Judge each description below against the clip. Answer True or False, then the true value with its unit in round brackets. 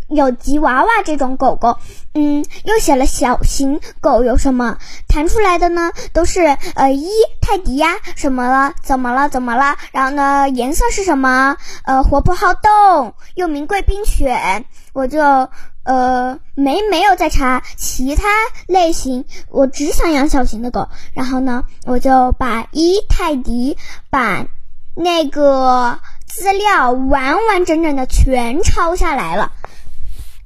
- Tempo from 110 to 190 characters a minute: False (200 characters per minute)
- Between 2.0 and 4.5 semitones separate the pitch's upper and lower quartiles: False (5.2 semitones)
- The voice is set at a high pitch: True (285 Hz)